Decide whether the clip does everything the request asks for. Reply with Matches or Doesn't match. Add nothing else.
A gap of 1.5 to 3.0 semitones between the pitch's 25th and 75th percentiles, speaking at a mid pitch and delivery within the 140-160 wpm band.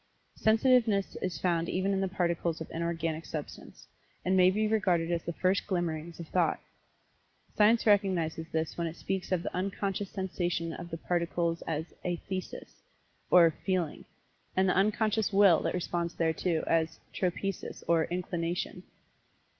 Matches